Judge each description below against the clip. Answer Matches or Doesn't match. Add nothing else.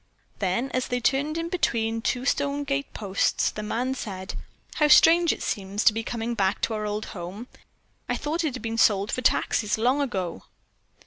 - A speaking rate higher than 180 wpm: Matches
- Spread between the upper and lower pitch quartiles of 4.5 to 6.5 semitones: Matches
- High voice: Matches